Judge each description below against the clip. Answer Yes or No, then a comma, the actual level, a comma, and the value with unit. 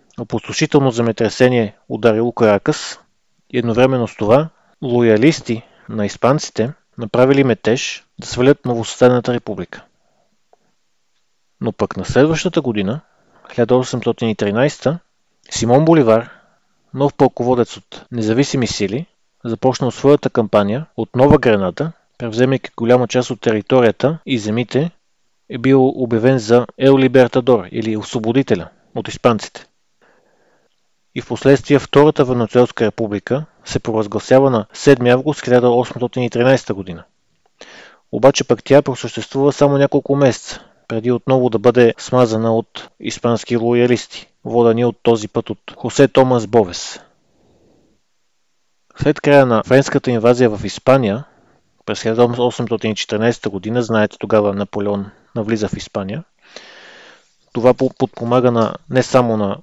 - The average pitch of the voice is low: Yes, low, 120 Hz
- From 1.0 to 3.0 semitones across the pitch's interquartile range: Yes, average, 2.7 semitones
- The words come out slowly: Yes, slow, 110 wpm